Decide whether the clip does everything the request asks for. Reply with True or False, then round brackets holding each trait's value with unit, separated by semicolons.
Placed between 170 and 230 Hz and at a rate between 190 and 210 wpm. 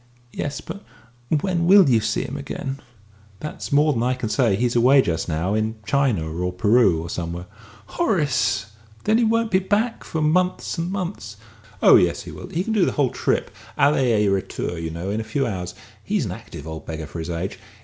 False (120 Hz; 205 wpm)